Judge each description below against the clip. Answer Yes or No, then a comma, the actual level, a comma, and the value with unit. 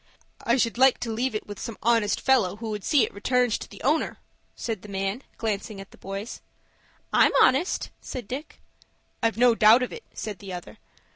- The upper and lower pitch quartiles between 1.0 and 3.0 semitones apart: No, average, 3.5 semitones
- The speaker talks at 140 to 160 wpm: No, average, 200 wpm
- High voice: Yes, high, 225 Hz